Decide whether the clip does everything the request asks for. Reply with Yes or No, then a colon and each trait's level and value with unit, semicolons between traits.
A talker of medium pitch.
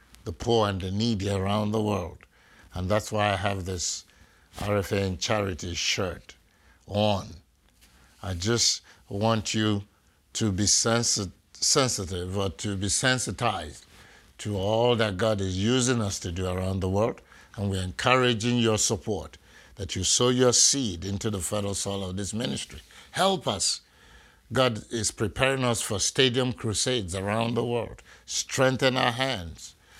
No: low, 105 Hz